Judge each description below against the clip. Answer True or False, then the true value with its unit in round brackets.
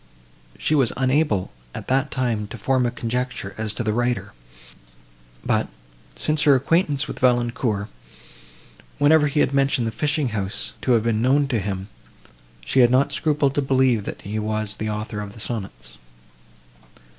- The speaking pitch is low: True (120 Hz)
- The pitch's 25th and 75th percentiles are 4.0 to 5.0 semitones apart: True (4.3 semitones)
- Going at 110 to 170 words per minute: True (165 wpm)